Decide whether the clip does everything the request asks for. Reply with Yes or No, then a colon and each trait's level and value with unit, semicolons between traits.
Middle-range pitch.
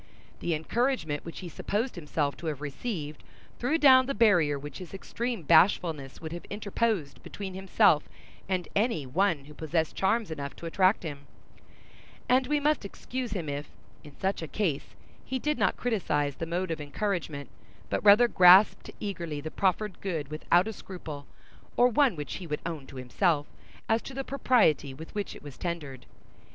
Yes: medium, 175 Hz